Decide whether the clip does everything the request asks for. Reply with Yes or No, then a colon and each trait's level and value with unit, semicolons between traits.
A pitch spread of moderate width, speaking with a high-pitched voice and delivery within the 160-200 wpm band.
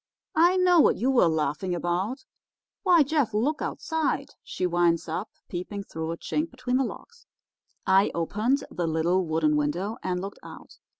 No: wide, 7.9 semitones; high, 195 Hz; average, 165 wpm